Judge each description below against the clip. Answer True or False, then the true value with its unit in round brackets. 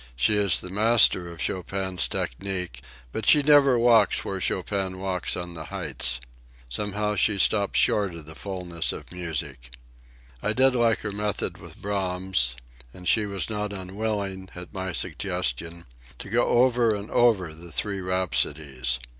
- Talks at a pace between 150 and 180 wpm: True (155 wpm)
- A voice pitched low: True (95 Hz)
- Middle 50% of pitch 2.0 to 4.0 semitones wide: True (3.4 semitones)